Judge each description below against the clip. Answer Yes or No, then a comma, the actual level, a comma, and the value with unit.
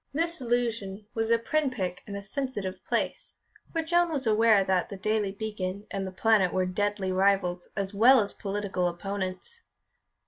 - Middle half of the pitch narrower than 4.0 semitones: Yes, average, 3.4 semitones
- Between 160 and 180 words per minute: Yes, average, 170 wpm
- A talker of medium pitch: No, high, 205 Hz